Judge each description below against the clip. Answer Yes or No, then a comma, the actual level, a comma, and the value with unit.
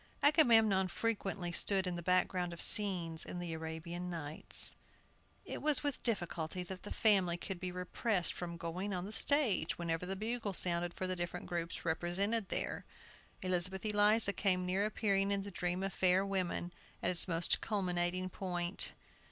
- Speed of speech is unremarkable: Yes, average, 165 wpm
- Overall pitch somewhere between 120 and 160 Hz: No, medium, 185 Hz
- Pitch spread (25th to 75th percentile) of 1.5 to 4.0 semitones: Yes, narrow, 2.5 semitones